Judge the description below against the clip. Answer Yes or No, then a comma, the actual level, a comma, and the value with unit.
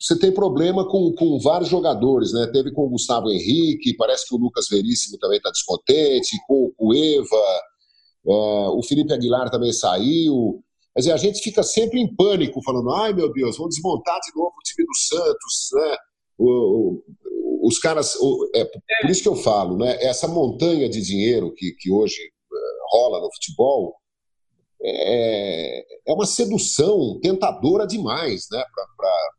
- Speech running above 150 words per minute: Yes, average, 170 wpm